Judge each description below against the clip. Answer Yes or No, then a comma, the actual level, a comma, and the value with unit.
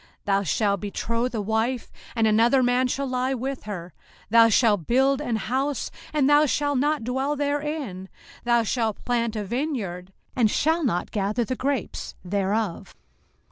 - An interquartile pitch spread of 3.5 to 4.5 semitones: Yes, average, 4.2 semitones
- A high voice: Yes, high, 240 Hz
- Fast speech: No, average, 160 wpm